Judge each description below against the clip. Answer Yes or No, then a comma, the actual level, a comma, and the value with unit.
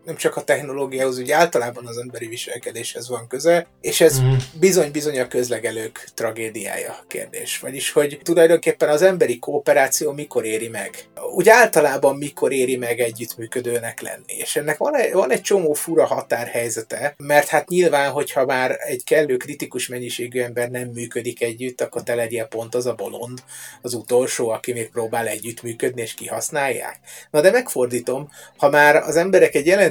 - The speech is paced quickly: Yes, fast, 160 wpm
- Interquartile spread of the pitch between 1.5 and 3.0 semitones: No, average, 4.1 semitones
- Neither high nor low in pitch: No, low, 125 Hz